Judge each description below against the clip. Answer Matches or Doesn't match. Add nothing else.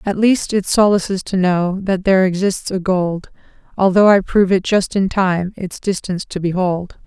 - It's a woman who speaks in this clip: Matches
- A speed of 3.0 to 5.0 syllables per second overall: Matches